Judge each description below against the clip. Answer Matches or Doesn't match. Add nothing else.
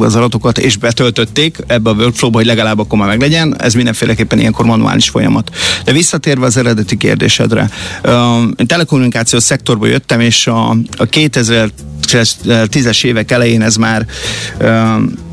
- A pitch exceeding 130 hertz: Doesn't match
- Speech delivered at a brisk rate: Doesn't match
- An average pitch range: Doesn't match